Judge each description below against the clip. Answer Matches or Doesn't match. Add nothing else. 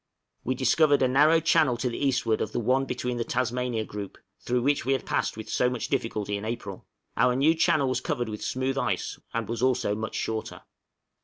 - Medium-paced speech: Doesn't match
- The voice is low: Matches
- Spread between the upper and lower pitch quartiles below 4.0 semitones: Matches